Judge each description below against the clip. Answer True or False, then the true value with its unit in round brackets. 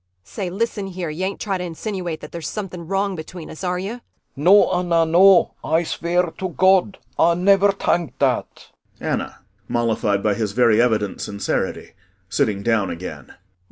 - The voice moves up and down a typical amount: False (7.4 semitones)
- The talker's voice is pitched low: False (175 Hz)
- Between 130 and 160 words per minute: False (170 wpm)